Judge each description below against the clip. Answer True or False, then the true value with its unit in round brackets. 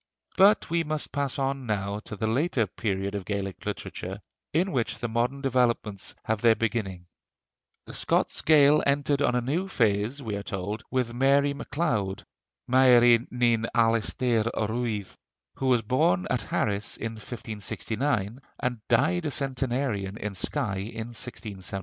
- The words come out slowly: False (150 wpm)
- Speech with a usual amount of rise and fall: True (4.5 semitones)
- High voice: False (120 Hz)